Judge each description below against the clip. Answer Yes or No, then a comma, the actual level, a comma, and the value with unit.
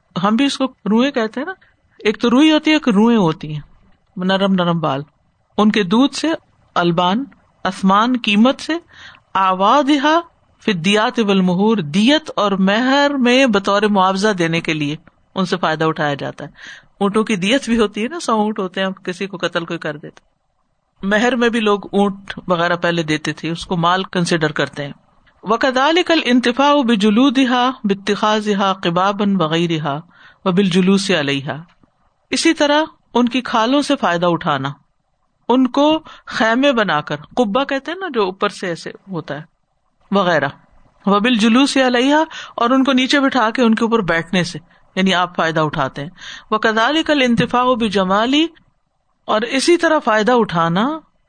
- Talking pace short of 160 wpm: No, average, 165 wpm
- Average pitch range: No, wide, 6.4 semitones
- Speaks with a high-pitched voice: Yes, high, 210 Hz